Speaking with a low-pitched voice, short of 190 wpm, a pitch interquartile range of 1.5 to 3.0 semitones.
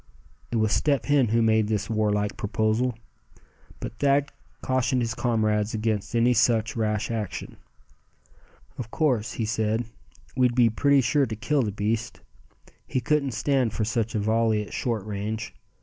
Yes: low, 115 Hz; average, 160 wpm; average, 2.7 semitones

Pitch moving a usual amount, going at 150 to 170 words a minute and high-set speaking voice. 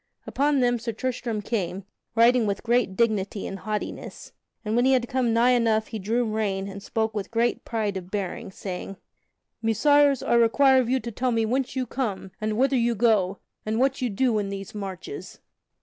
No: average, 3.4 semitones; average, 195 wpm; high, 225 Hz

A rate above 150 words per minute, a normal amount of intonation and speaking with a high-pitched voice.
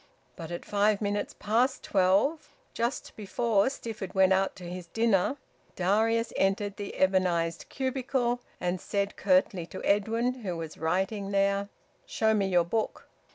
No: average, 145 wpm; average, 3.4 semitones; high, 200 Hz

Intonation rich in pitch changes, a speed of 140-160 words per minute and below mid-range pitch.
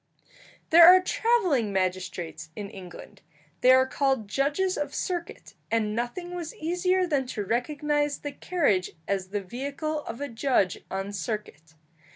No: wide, 7.7 semitones; average, 145 wpm; very high, 260 Hz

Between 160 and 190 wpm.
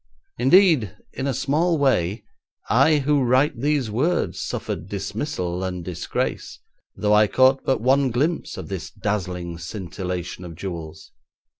No: slow, 135 wpm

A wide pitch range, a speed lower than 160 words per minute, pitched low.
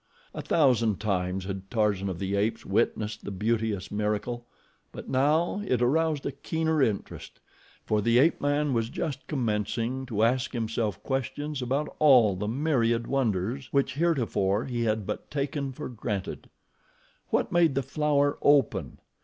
No: average, 4.9 semitones; average, 150 wpm; low, 120 Hz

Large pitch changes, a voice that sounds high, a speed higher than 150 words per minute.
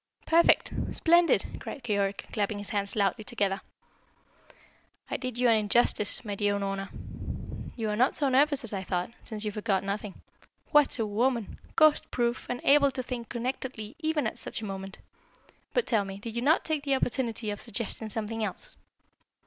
No: average, 4.2 semitones; high, 225 Hz; average, 175 wpm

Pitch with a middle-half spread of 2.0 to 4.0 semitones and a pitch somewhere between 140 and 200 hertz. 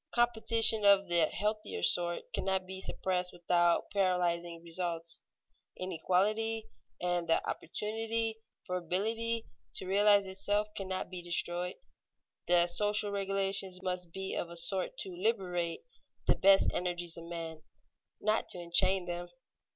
Yes: average, 2.8 semitones; medium, 185 Hz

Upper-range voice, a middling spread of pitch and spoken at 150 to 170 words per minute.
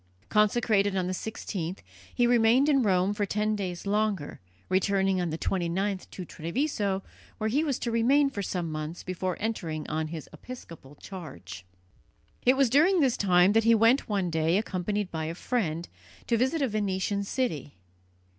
Yes: high, 200 Hz; average, 4.6 semitones; average, 165 wpm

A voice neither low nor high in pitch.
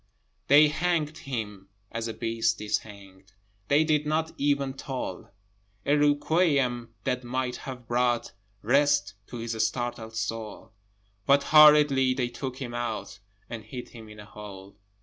No: low, 125 Hz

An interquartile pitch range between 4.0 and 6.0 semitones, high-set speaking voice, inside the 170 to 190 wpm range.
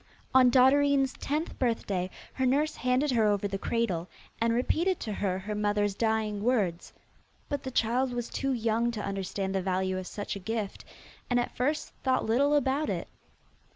Yes: average, 4.4 semitones; high, 230 Hz; average, 175 wpm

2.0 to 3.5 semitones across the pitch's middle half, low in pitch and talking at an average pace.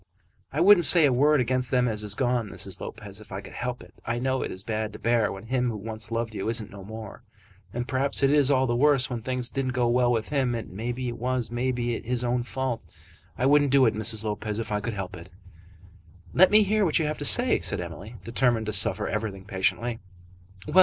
No: average, 3.2 semitones; low, 120 Hz; fast, 230 wpm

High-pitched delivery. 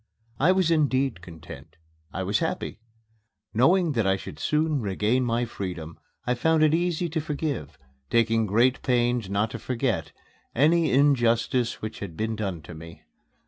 No: low, 120 Hz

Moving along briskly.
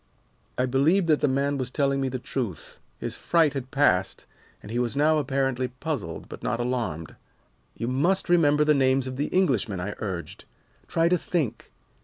No: average, 180 wpm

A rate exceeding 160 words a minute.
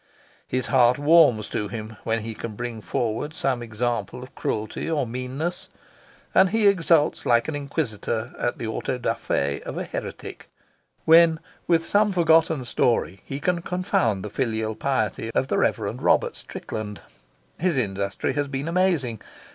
No: average, 145 wpm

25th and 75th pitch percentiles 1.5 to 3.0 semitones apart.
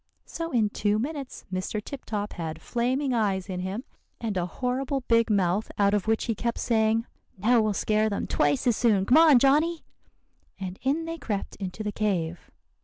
No: average, 4.2 semitones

